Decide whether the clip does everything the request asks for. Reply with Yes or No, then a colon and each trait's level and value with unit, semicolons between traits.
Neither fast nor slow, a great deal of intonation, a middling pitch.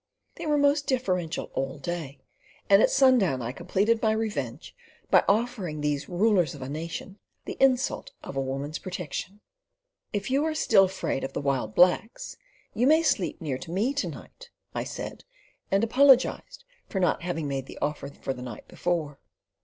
Yes: average, 170 wpm; wide, 8.2 semitones; medium, 180 Hz